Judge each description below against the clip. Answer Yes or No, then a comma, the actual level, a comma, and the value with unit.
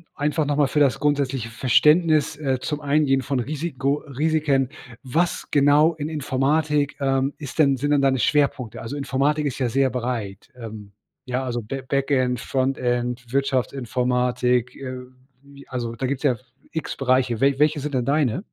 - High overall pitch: No, low, 135 Hz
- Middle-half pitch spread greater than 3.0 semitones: No, narrow, 2.6 semitones